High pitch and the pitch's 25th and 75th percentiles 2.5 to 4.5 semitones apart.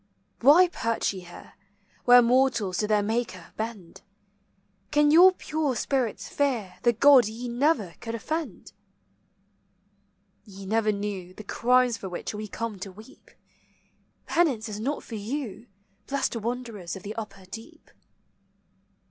Yes: high, 230 Hz; average, 4.0 semitones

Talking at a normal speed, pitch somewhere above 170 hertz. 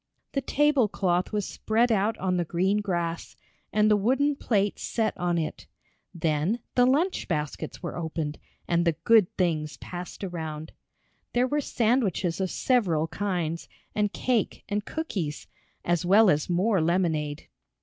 Yes: average, 150 wpm; medium, 185 Hz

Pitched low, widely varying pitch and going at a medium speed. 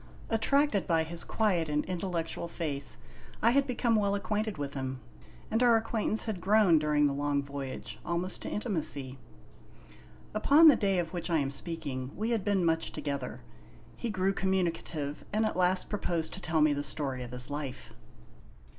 No: medium, 170 Hz; wide, 6.2 semitones; average, 170 wpm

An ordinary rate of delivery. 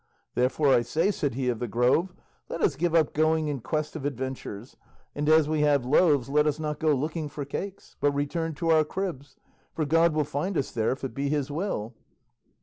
No: fast, 215 wpm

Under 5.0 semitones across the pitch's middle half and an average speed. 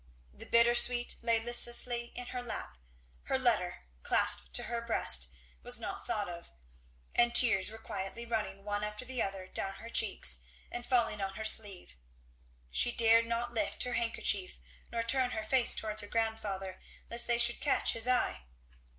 Yes: average, 3.3 semitones; average, 170 wpm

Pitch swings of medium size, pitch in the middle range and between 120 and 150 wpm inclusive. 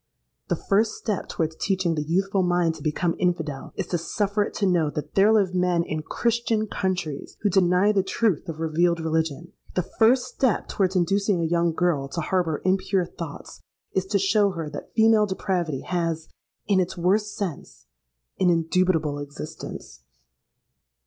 No: average, 3.4 semitones; medium, 180 Hz; average, 160 wpm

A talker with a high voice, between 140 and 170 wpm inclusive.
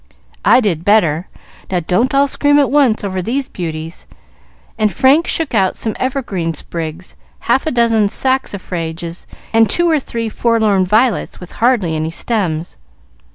Yes: high, 215 Hz; average, 150 wpm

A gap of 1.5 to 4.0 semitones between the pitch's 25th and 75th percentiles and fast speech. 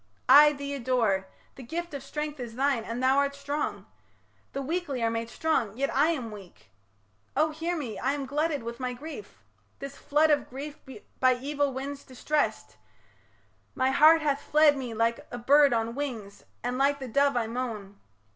No: average, 3.6 semitones; average, 180 wpm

